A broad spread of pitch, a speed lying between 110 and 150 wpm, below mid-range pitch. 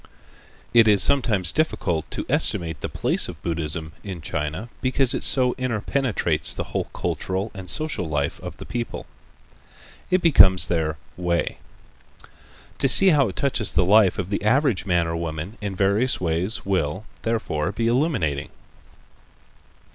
Yes: wide, 6.2 semitones; average, 145 wpm; very low, 95 Hz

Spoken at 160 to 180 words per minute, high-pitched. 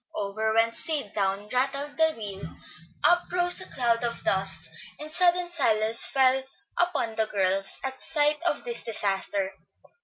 No: average, 150 wpm; high, 240 Hz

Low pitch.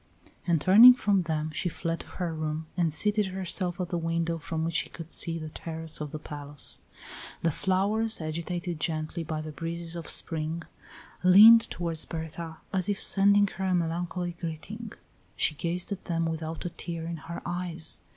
No: medium, 170 Hz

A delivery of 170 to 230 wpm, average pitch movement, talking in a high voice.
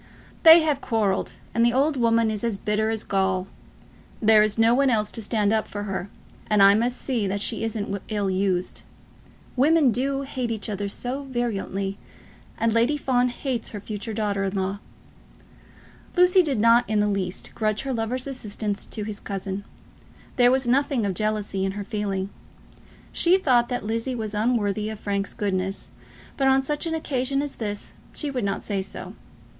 Yes: average, 180 wpm; average, 3.9 semitones; high, 220 Hz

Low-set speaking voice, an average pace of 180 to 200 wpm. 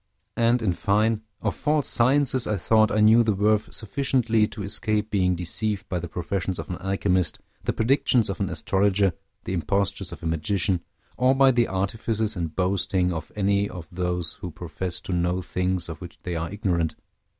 Yes: low, 100 Hz; average, 185 wpm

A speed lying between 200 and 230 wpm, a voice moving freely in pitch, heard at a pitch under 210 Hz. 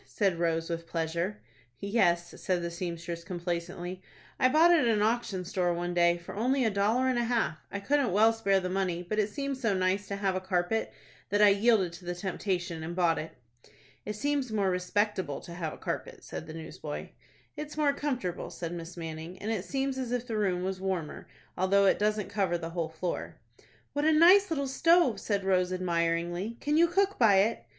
No: fast, 205 wpm; average, 4.8 semitones; high, 190 Hz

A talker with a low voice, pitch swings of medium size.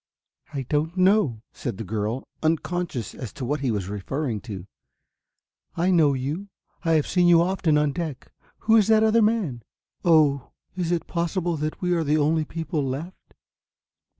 No: medium, 155 Hz; average, 4.9 semitones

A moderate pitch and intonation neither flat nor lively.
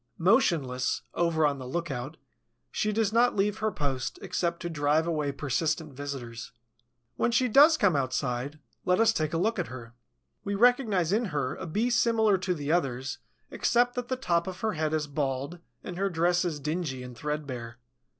No: medium, 165 Hz; wide, 6.6 semitones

